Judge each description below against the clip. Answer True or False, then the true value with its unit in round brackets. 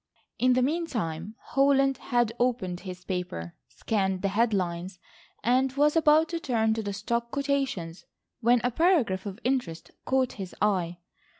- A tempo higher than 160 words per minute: False (155 wpm)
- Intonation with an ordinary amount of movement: False (6.1 semitones)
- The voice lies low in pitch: False (230 Hz)